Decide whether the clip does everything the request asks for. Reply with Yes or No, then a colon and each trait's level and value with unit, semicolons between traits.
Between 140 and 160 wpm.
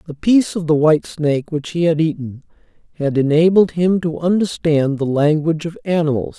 No: average, 180 wpm